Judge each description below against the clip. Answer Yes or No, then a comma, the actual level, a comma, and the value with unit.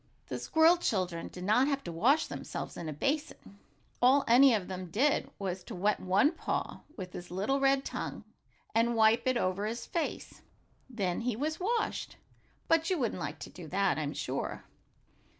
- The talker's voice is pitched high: Yes, high, 225 Hz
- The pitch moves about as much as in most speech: No, wide, 6.9 semitones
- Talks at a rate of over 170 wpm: Yes, average, 180 wpm